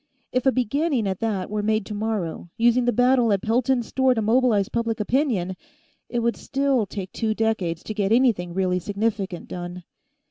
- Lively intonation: No, average, 4.0 semitones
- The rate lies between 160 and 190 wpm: Yes, average, 175 wpm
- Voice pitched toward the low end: No, high, 220 Hz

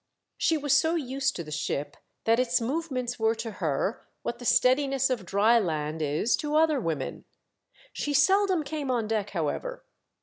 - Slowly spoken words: No, average, 170 wpm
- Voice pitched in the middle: No, high, 245 Hz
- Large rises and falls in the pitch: Yes, wide, 6.4 semitones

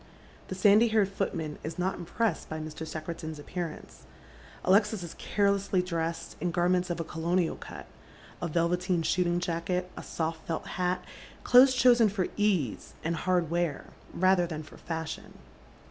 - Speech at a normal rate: Yes, average, 150 wpm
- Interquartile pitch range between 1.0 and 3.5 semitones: Yes, narrow, 2.6 semitones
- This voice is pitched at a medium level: Yes, medium, 175 Hz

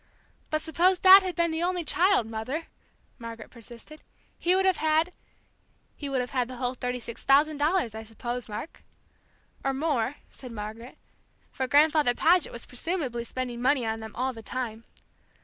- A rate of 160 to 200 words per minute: Yes, average, 175 wpm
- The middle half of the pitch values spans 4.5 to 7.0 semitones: Yes, average, 5.3 semitones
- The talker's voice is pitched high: Yes, very high, 260 Hz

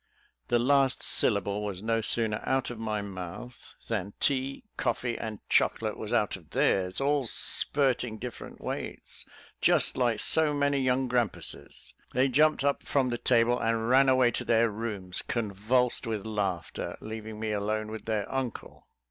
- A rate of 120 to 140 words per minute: No, average, 155 wpm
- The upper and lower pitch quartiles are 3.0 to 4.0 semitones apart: Yes, average, 3.3 semitones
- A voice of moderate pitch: No, low, 115 Hz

